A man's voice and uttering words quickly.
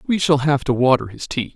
Yes: male; fast, 270 wpm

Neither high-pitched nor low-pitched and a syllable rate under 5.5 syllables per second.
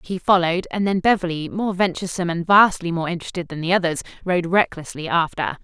No: medium, 175 Hz; 6.3 syllables/s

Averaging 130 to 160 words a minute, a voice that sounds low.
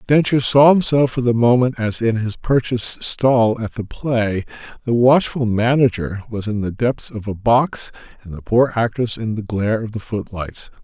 No: average, 190 wpm; low, 115 Hz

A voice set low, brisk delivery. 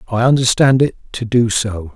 No: low, 120 Hz; average, 185 wpm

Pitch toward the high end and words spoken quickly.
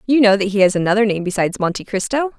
Yes: high, 210 Hz; fast, 250 wpm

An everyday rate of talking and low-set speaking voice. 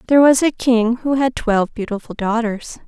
No: average, 190 wpm; high, 235 Hz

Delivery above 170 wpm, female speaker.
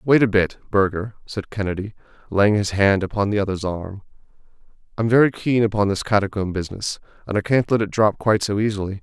No: average, 200 wpm; male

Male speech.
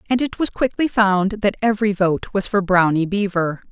No: female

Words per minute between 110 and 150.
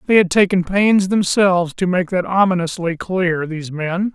No: average, 175 wpm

